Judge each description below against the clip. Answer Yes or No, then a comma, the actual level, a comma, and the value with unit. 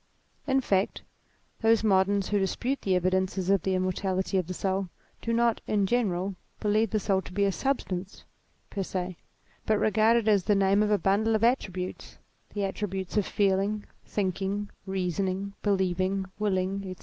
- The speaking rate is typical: Yes, average, 170 wpm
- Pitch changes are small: Yes, narrow, 1.9 semitones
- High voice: Yes, high, 195 Hz